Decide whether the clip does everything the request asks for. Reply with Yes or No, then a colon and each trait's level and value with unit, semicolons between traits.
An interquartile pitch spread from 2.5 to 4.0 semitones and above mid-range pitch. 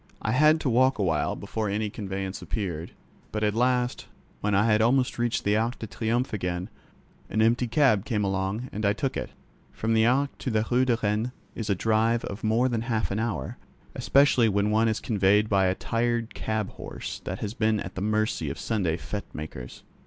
No: average, 2.8 semitones; low, 110 Hz